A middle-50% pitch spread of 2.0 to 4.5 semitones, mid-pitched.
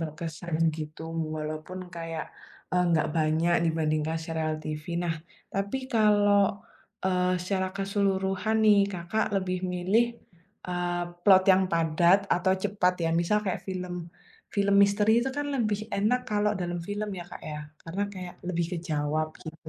Yes: average, 3.5 semitones; medium, 180 Hz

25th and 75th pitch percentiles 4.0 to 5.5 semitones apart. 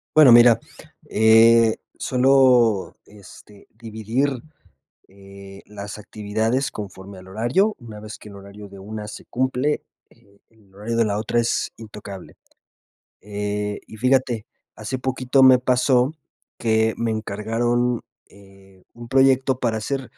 No: average, 3.5 semitones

